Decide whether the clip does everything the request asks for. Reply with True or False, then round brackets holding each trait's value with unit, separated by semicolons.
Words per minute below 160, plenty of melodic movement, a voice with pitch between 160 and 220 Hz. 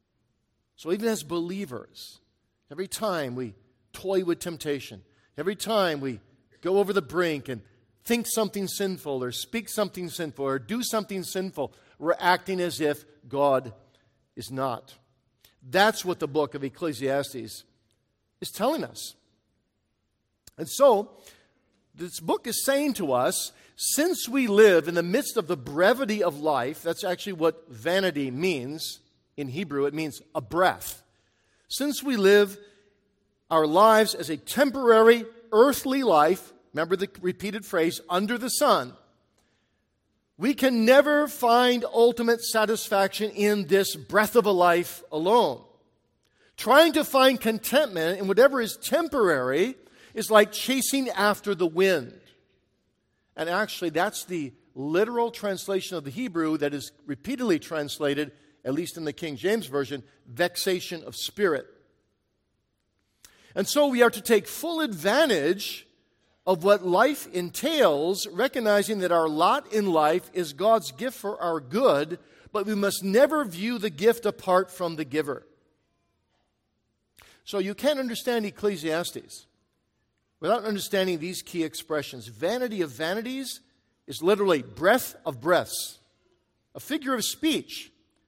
True (135 wpm; 7.1 semitones; 185 Hz)